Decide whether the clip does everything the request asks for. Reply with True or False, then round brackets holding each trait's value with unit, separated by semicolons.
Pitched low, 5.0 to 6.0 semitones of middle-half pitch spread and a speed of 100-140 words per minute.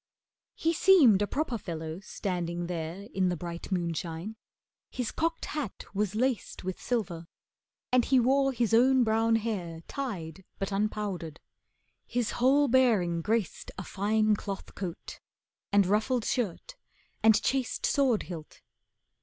False (210 Hz; 5.6 semitones; 135 wpm)